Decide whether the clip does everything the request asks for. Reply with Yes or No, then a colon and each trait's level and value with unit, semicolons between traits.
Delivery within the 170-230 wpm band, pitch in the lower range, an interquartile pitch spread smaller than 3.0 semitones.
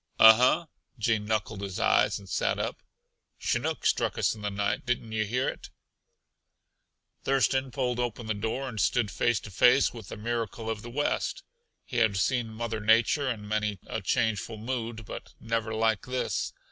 Yes: average, 175 wpm; low, 115 Hz; narrow, 2.4 semitones